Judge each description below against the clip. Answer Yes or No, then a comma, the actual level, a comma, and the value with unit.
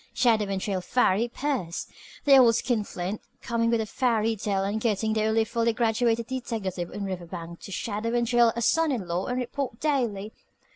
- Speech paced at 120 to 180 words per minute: No, average, 190 wpm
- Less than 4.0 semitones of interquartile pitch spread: Yes, average, 3.2 semitones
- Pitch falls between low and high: No, high, 225 Hz